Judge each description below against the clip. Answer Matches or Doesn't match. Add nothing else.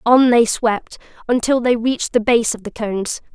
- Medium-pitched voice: Doesn't match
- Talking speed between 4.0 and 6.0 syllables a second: Matches